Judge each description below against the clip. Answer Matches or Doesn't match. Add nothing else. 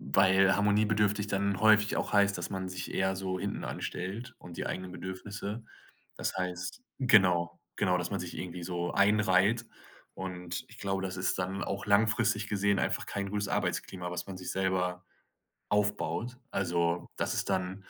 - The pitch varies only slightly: Matches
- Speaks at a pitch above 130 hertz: Doesn't match